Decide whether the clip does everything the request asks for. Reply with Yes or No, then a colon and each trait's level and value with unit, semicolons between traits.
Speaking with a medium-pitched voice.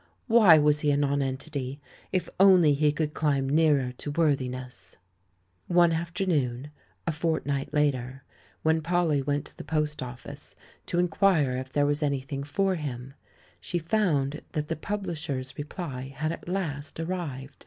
Yes: medium, 150 Hz